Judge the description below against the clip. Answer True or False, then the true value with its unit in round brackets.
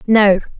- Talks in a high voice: True (205 Hz)